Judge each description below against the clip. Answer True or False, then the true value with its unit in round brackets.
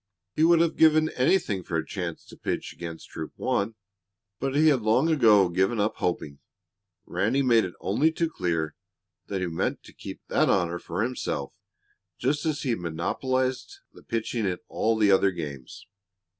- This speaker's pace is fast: False (175 wpm)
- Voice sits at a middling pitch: False (110 Hz)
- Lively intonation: True (7.4 semitones)